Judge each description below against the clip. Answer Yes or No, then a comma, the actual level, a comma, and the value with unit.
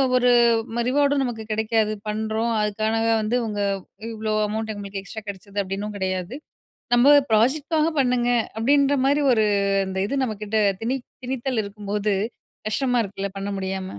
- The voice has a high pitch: Yes, high, 220 Hz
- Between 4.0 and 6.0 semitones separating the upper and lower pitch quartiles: No, average, 3.5 semitones